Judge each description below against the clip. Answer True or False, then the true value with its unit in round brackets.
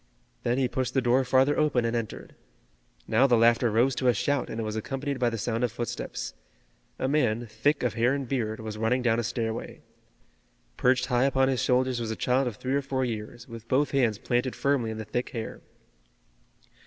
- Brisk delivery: True (210 wpm)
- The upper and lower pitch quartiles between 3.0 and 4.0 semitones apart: False (2.5 semitones)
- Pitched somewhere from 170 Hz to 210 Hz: False (125 Hz)